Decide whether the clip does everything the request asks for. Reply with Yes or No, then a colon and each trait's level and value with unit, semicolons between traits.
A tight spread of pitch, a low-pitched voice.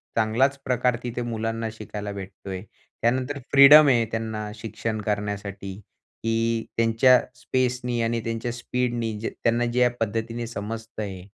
Yes: narrow, 2.1 semitones; low, 115 Hz